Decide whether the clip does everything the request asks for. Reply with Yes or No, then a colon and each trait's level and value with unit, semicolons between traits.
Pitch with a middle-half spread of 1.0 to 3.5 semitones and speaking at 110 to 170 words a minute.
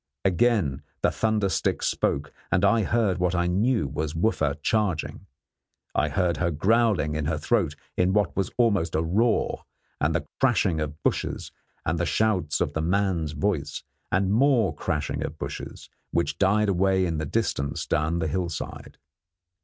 No: average, 5.0 semitones; average, 160 wpm